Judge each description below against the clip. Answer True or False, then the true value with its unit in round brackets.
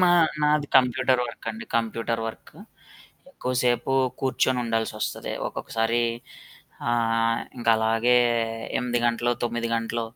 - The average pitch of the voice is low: True (120 Hz)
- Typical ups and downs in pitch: False (1.7 semitones)